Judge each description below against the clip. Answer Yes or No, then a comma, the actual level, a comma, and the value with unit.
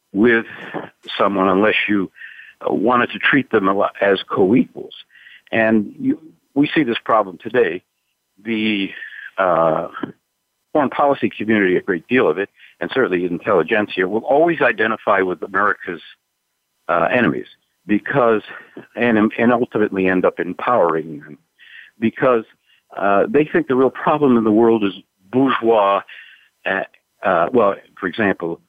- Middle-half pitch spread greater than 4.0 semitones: No, average, 3.5 semitones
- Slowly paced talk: Yes, slow, 130 wpm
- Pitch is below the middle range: Yes, low, 110 Hz